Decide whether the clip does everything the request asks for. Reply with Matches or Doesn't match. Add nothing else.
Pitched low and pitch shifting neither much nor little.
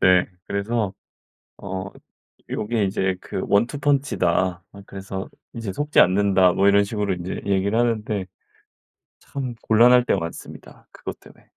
Matches